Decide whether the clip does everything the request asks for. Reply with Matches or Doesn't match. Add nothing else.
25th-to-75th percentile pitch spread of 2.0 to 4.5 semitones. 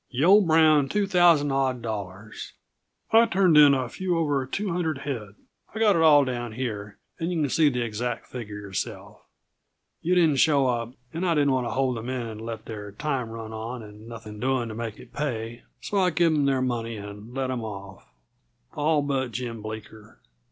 Doesn't match